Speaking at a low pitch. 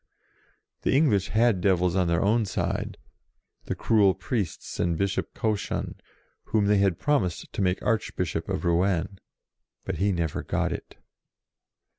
Yes: very low, 95 Hz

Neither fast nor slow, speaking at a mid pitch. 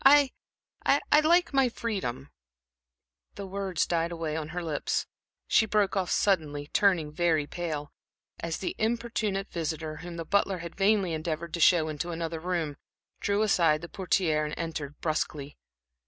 Yes: average, 155 wpm; medium, 170 Hz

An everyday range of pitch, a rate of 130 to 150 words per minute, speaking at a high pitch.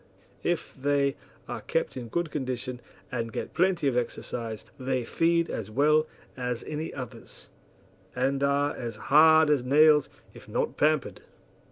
No: average, 3.7 semitones; average, 145 wpm; medium, 140 Hz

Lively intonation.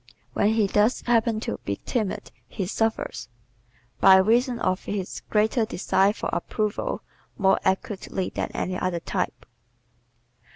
No: average, 2.9 semitones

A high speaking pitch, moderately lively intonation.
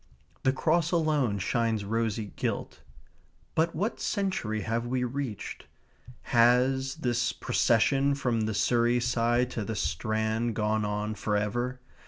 No: low, 120 Hz; average, 3.3 semitones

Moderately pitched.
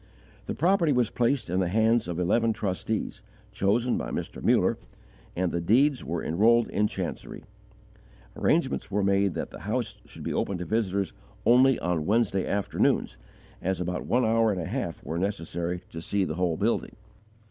No: low, 100 Hz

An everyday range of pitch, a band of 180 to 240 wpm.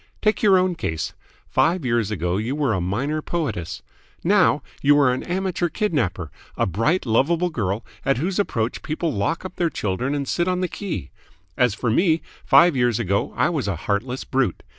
No: wide, 8.1 semitones; average, 185 wpm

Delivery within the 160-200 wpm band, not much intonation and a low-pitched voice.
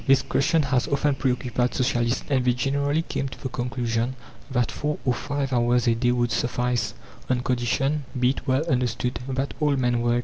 Yes: average, 190 wpm; narrow, 2.0 semitones; low, 125 Hz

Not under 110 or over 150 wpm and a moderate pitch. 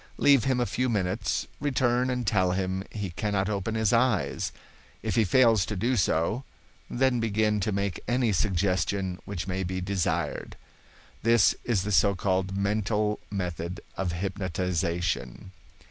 No: average, 145 wpm; low, 100 Hz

